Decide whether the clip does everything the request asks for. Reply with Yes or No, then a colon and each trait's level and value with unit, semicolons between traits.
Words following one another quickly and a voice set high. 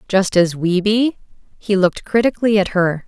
No: average, 175 wpm; high, 200 Hz